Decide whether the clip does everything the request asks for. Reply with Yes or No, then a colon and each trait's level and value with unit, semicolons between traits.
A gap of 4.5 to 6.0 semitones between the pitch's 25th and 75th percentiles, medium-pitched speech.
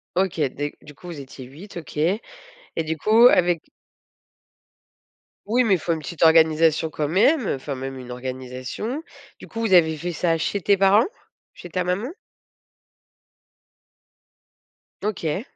Yes: average, 4.8 semitones; medium, 165 Hz